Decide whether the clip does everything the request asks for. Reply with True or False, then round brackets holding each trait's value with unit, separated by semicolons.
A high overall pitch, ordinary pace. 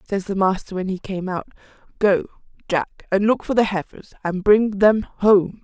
True (195 Hz; 190 wpm)